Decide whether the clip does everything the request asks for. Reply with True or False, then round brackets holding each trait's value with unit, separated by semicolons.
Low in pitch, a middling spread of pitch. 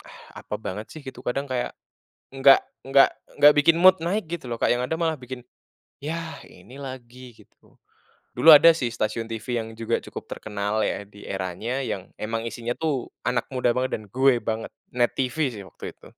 True (125 Hz; 3.6 semitones)